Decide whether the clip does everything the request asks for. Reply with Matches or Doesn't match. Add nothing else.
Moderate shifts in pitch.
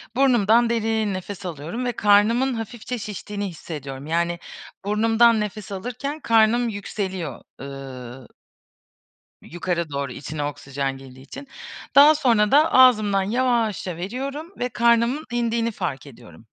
Doesn't match